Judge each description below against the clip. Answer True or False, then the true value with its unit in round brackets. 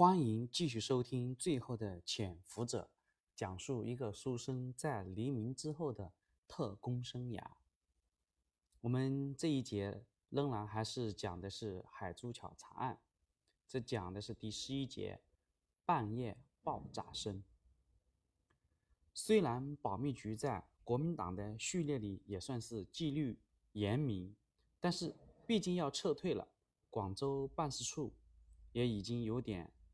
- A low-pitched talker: True (110 Hz)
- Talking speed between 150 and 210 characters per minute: True (190 characters per minute)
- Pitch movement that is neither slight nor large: False (6.0 semitones)